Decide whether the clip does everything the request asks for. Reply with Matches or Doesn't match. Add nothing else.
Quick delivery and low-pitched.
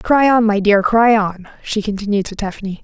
Doesn't match